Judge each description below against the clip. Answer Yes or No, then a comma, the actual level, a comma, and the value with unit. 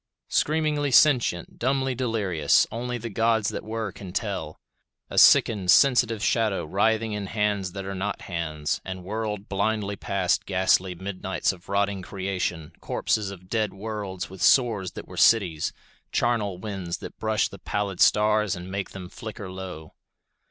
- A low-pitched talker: Yes, low, 100 Hz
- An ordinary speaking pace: Yes, average, 150 wpm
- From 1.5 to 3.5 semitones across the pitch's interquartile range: Yes, average, 3.1 semitones